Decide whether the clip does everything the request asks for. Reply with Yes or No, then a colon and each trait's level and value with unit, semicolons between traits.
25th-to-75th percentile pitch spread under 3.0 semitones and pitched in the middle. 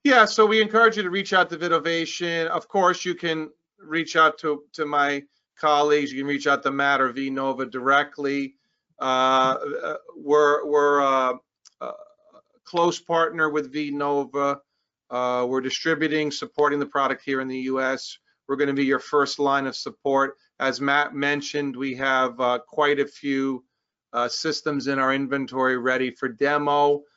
Yes: narrow, 2.6 semitones; medium, 145 Hz